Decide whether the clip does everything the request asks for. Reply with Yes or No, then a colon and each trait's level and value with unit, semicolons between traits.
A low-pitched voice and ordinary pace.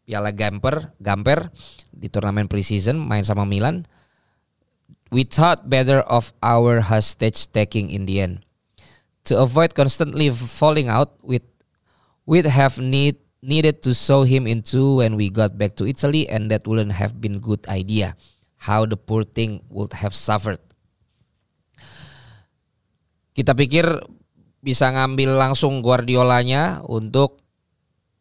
Yes: low, 120 Hz; average, 130 wpm